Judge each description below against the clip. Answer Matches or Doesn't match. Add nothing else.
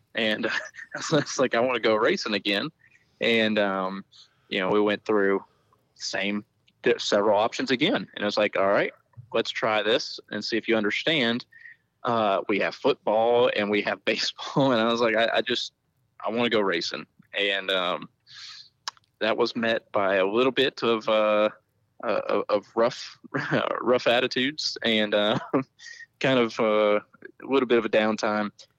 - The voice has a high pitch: Doesn't match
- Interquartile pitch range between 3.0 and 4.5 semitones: Doesn't match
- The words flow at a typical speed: Matches